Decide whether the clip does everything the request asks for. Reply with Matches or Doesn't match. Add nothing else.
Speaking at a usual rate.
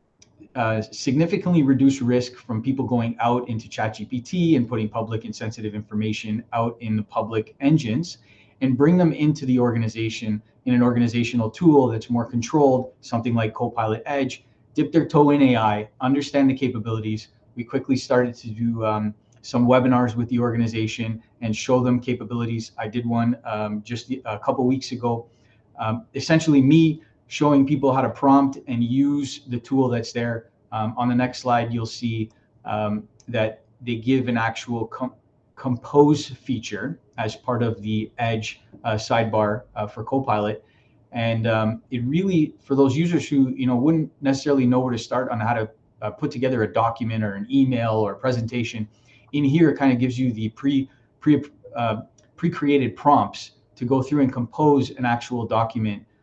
Matches